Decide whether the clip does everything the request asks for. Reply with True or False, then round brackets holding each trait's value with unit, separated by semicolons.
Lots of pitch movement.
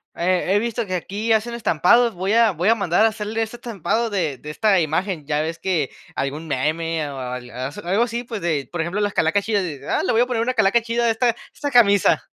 True (5.8 semitones)